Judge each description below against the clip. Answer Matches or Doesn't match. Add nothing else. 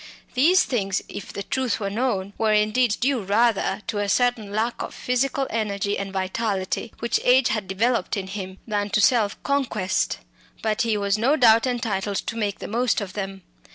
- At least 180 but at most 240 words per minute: Matches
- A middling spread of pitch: Matches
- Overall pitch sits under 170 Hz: Doesn't match